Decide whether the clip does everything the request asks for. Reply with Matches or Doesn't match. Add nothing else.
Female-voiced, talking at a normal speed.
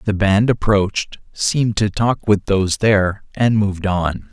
Doesn't match